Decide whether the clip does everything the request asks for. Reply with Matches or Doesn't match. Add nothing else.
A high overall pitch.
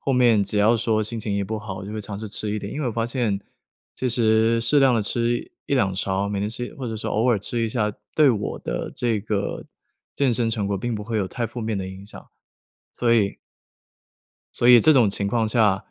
Doesn't match